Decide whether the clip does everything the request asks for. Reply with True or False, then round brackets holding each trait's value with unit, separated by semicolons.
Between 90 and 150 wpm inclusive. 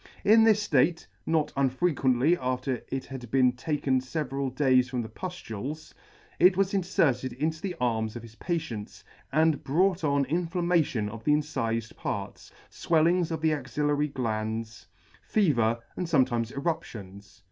True (145 wpm)